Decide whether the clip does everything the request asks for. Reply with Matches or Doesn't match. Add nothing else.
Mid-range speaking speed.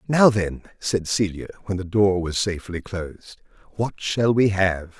Matches